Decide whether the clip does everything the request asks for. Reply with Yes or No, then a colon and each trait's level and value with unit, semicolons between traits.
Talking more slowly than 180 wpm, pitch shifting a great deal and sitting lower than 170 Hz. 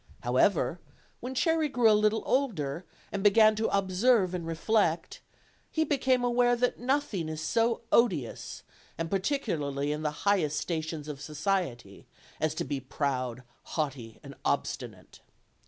No: average, 140 wpm; wide, 7.7 semitones; medium, 185 Hz